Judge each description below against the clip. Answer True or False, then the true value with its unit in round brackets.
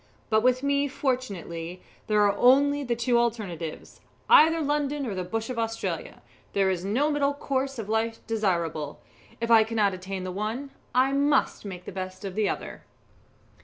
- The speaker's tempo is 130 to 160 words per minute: False (170 wpm)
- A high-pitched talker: True (225 Hz)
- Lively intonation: True (5.9 semitones)